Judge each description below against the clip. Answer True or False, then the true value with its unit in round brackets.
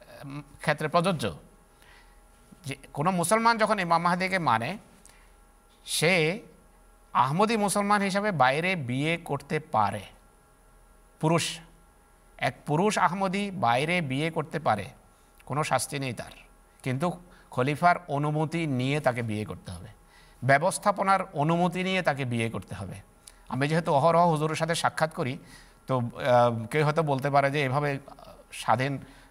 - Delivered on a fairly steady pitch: False (5.3 semitones)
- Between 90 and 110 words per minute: False (120 wpm)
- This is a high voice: False (145 Hz)